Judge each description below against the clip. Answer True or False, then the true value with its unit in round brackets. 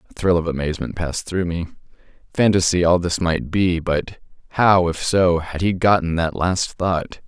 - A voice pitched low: True (85 Hz)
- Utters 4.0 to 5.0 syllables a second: True (4.9 syllables/s)